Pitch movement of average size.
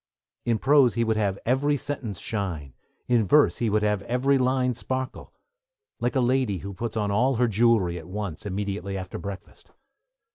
Yes: average, 4.3 semitones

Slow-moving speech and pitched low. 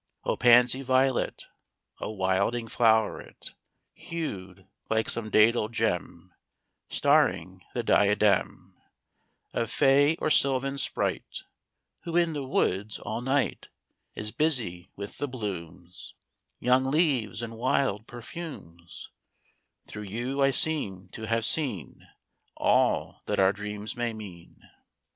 Yes: slow, 115 wpm; low, 115 Hz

